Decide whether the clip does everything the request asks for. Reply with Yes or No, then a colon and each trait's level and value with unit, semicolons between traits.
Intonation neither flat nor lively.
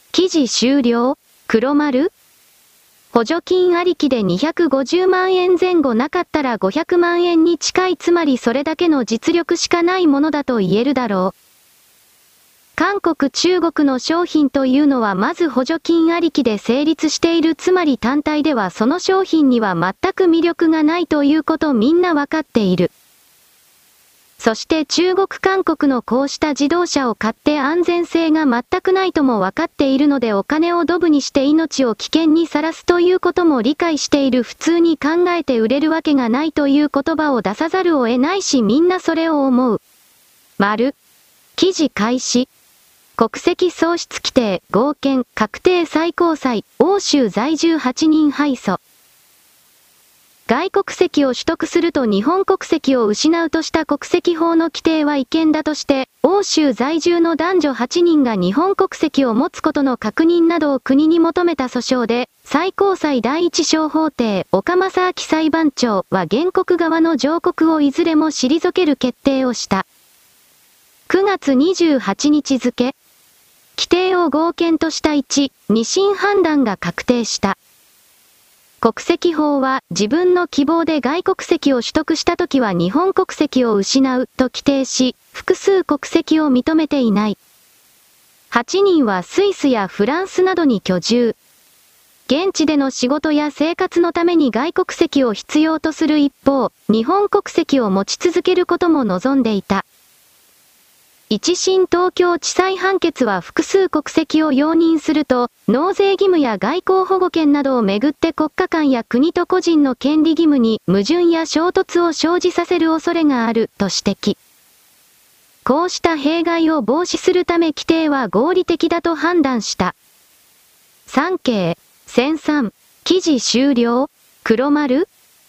Yes: average, 4.9 semitones